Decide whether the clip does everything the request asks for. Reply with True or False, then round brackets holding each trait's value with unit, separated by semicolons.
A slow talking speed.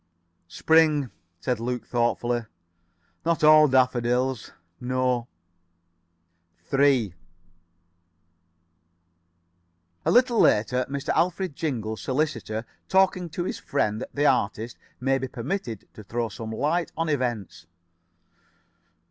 True (95 wpm)